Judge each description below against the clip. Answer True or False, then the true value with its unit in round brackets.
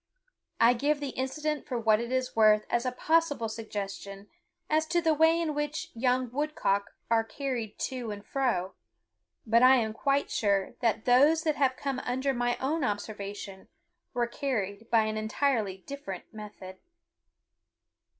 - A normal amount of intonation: True (4.6 semitones)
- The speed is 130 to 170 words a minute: True (155 wpm)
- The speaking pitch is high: True (245 Hz)